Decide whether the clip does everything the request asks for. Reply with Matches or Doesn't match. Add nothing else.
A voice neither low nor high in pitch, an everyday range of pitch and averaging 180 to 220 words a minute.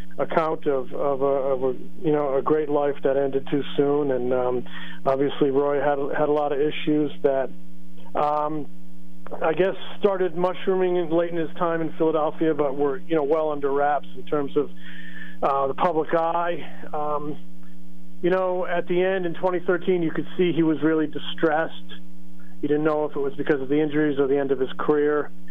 Matches